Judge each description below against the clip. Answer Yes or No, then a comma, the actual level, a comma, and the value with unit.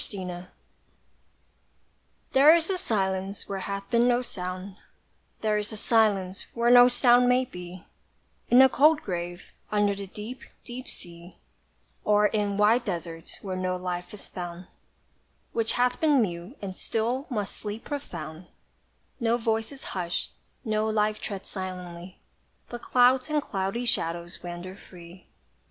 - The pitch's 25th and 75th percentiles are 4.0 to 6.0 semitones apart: Yes, average, 4.7 semitones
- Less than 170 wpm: Yes, average, 140 wpm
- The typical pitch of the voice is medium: No, high, 205 Hz